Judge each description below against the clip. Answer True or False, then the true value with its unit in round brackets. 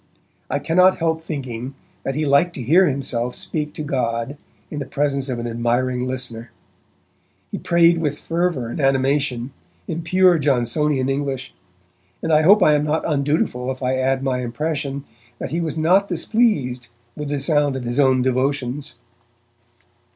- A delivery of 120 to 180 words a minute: True (160 wpm)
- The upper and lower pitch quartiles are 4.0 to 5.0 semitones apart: False (3.5 semitones)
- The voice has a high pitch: False (140 Hz)